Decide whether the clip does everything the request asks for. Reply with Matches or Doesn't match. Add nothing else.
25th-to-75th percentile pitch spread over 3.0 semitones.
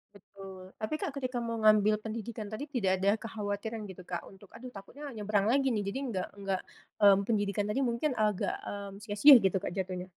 Doesn't match